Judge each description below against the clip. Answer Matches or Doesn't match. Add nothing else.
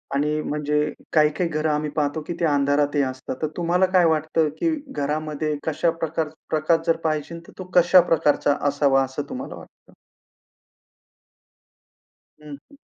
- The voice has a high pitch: Doesn't match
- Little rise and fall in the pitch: Matches